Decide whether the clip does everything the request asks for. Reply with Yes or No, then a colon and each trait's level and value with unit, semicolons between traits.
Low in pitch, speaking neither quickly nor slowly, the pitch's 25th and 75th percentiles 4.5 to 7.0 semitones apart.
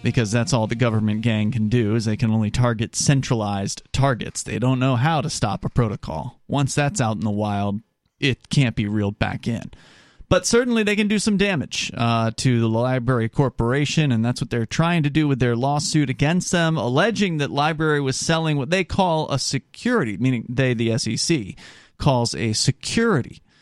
Yes: low, 130 Hz; average, 195 wpm; average, 4.9 semitones